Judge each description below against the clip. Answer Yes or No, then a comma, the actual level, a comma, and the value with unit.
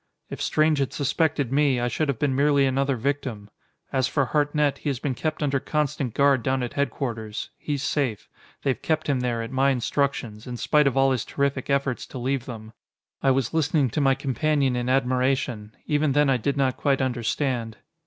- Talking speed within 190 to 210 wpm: Yes, average, 195 wpm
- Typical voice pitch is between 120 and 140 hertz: Yes, low, 135 Hz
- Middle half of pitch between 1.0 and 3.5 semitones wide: Yes, narrow, 2.4 semitones